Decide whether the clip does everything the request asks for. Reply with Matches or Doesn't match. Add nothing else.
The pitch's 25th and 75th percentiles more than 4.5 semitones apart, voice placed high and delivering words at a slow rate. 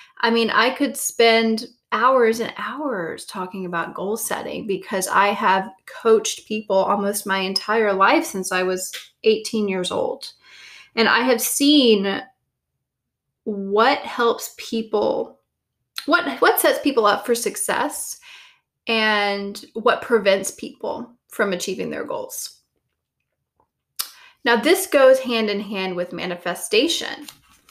Matches